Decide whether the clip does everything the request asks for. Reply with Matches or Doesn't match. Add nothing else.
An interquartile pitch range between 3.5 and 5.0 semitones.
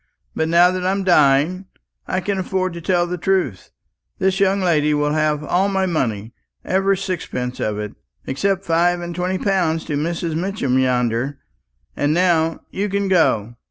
Matches